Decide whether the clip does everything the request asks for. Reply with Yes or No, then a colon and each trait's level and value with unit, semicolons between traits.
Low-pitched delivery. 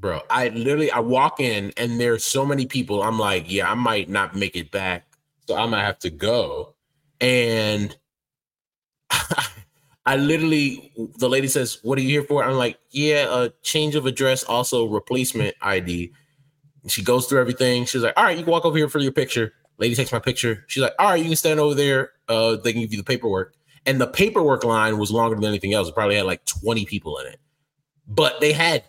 Yes: low, 130 Hz